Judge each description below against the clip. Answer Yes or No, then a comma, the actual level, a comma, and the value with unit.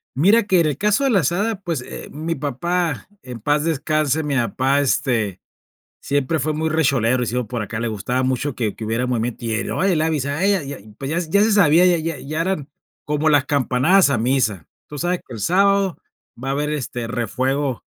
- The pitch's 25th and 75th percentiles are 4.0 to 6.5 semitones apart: Yes, average, 4.9 semitones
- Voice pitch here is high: No, medium, 145 Hz